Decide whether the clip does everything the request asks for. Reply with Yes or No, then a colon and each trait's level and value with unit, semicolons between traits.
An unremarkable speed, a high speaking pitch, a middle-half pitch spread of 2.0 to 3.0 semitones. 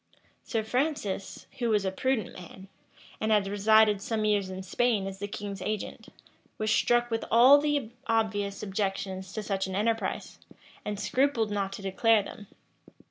Yes: average, 160 wpm; high, 210 Hz; narrow, 2.6 semitones